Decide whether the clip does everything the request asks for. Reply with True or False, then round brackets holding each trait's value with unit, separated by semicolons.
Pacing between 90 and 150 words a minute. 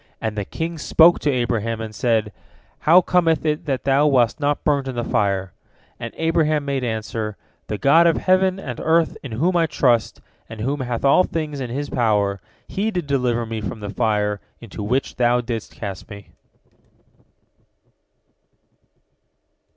False (165 wpm)